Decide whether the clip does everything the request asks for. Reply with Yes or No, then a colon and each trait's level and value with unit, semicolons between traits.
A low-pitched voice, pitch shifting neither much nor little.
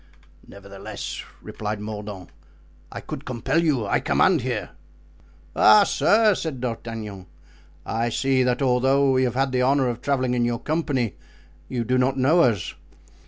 Yes: low, 125 Hz; average, 3.4 semitones